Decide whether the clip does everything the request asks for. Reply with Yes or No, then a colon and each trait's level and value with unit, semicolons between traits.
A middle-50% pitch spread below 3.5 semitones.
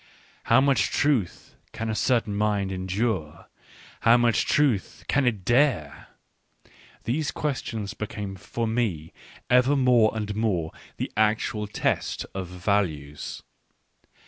No: average, 4.1 semitones